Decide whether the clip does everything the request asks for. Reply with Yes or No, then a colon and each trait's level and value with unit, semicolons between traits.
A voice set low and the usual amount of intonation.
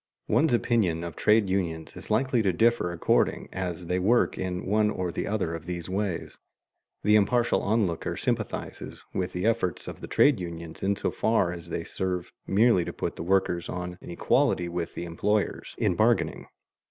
Yes: very low, 95 Hz; average, 3.7 semitones